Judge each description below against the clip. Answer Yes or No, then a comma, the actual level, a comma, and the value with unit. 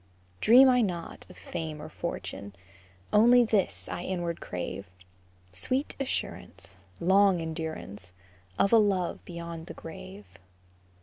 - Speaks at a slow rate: Yes, slow, 120 wpm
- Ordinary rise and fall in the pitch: Yes, average, 4.8 semitones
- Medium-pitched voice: Yes, medium, 170 Hz